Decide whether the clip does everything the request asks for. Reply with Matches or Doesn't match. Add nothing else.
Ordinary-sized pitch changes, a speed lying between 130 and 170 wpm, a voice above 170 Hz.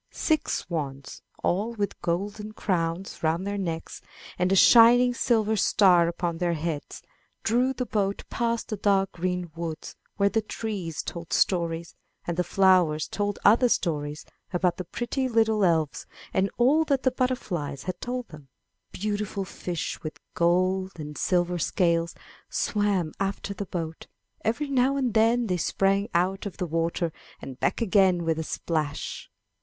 Matches